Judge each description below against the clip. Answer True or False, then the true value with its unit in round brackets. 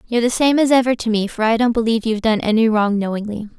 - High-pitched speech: True (225 Hz)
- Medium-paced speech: False (270 wpm)